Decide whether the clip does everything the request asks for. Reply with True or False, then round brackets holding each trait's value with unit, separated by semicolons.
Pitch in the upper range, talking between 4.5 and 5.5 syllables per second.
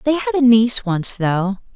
True (235 Hz; 5.2 syllables/s)